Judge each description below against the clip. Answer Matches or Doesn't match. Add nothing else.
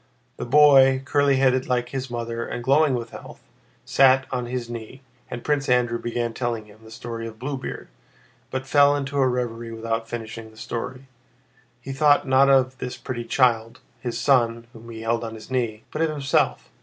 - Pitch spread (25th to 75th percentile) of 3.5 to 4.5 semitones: Doesn't match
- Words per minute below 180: Doesn't match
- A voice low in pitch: Matches